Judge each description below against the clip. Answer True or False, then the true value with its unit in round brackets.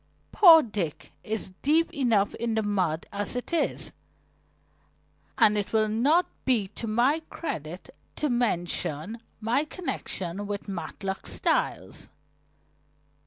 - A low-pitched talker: False (220 Hz)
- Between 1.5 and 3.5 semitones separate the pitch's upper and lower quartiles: False (5.1 semitones)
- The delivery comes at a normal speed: False (120 wpm)